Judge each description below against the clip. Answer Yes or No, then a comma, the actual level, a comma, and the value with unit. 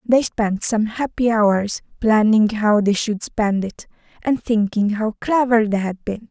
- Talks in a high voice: Yes, high, 220 Hz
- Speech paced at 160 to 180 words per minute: Yes, average, 170 wpm